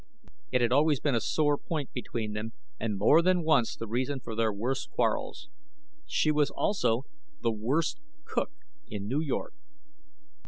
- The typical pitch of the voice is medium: No, low, 130 Hz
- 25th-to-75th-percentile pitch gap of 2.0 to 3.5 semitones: No, average, 5.2 semitones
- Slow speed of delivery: No, average, 160 wpm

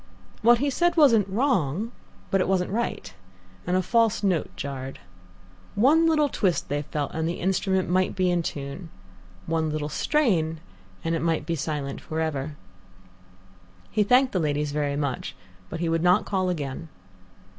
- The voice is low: No, medium, 175 Hz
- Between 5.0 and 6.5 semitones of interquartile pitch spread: Yes, wide, 5.5 semitones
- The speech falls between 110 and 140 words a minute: No, average, 165 wpm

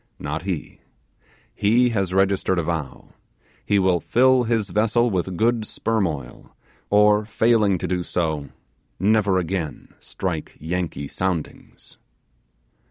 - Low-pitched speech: Yes, very low, 95 Hz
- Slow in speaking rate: Yes, slow, 120 wpm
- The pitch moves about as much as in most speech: Yes, average, 4.1 semitones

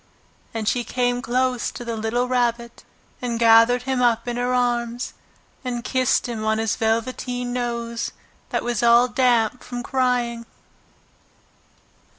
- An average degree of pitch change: No, narrow, 1.2 semitones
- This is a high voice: Yes, high, 240 Hz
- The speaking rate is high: No, average, 140 wpm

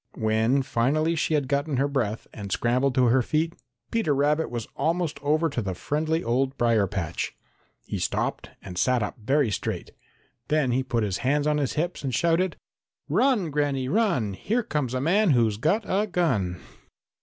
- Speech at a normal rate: Yes, average, 180 wpm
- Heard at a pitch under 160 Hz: Yes, medium, 140 Hz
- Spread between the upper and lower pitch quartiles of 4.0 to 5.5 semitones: Yes, average, 5.2 semitones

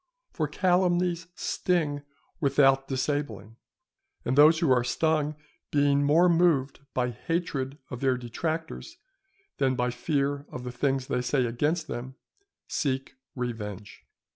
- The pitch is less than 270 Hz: Yes, medium, 140 Hz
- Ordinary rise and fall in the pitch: Yes, average, 4.1 semitones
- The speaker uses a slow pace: Yes, slow, 125 wpm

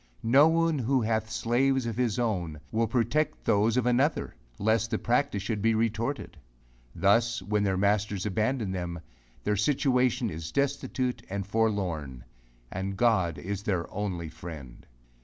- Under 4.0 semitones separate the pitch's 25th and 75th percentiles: No, average, 4.3 semitones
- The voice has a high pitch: No, low, 110 Hz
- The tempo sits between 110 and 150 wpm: Yes, average, 145 wpm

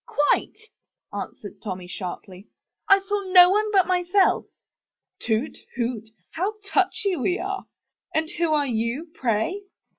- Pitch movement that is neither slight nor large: No, wide, 8.8 semitones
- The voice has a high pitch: Yes, very high, 340 Hz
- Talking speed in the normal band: No, slow, 125 wpm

